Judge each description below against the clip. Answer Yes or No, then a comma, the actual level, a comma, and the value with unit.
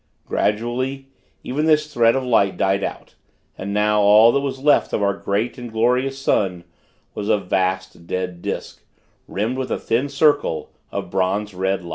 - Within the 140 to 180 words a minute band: Yes, average, 170 wpm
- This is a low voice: Yes, low, 110 Hz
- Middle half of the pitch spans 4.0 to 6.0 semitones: Yes, average, 5.3 semitones